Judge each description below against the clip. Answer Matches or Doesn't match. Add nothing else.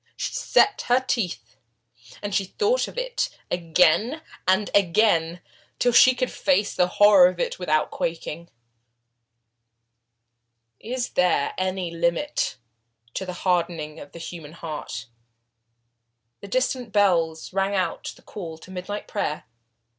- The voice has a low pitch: Doesn't match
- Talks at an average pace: Doesn't match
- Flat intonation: Doesn't match